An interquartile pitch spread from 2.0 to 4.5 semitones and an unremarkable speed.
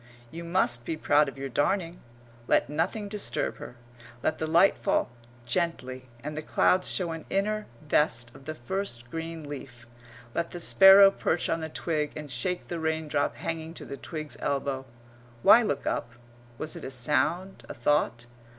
Yes: average, 4.1 semitones; average, 170 wpm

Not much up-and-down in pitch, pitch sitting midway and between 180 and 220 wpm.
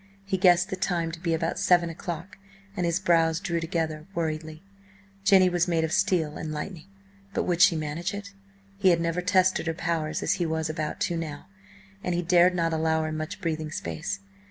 Yes: narrow, 2.3 semitones; medium, 170 Hz; average, 200 wpm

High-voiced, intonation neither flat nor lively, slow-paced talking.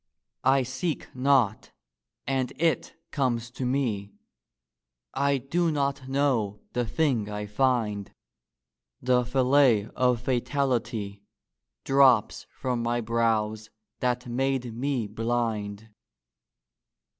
No: low, 125 Hz; average, 3.3 semitones; slow, 100 wpm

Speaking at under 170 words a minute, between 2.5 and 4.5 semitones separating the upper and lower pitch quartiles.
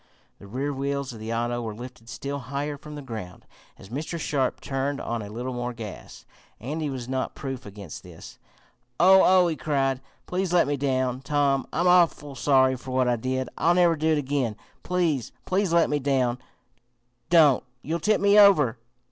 No: average, 185 wpm; average, 3.9 semitones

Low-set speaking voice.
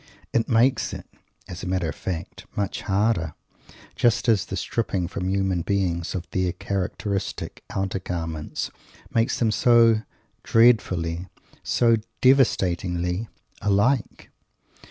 Yes: very low, 95 Hz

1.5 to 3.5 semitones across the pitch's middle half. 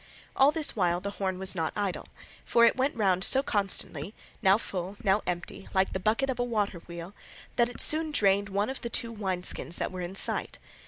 No: average, 4.0 semitones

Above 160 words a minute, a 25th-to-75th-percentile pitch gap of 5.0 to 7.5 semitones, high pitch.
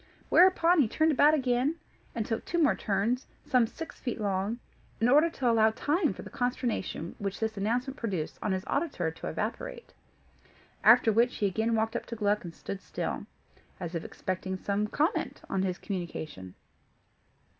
Yes: average, 170 wpm; wide, 5.6 semitones; high, 225 Hz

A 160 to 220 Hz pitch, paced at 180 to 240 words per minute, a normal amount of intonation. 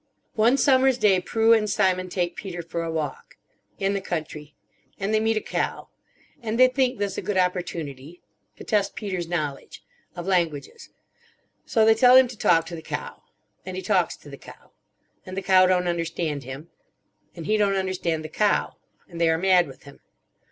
Yes: medium, 185 Hz; average, 190 wpm; average, 4.5 semitones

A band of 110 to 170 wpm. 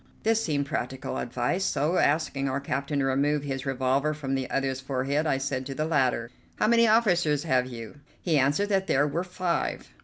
No: average, 190 wpm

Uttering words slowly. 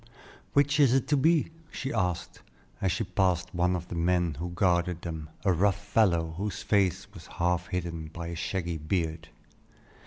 No: average, 175 wpm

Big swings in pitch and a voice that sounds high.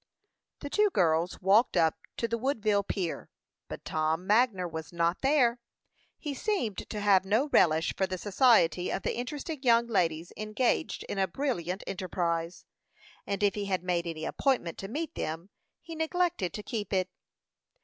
Yes: wide, 6.1 semitones; high, 200 Hz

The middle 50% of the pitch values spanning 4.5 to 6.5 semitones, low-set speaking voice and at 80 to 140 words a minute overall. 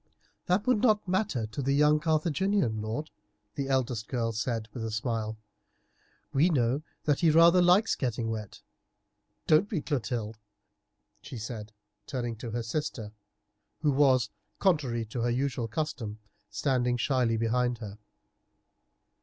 Yes: average, 5.2 semitones; low, 125 Hz; slow, 135 wpm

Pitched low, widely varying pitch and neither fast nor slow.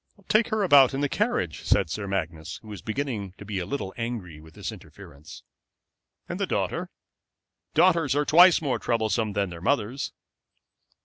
Yes: low, 110 Hz; wide, 7.1 semitones; average, 170 wpm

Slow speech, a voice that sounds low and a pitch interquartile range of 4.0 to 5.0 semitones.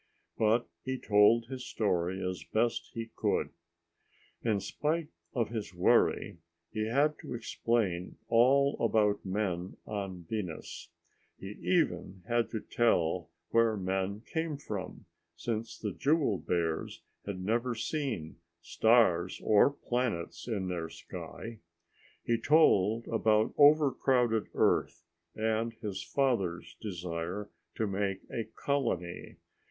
Yes: slow, 115 wpm; low, 110 Hz; average, 4.4 semitones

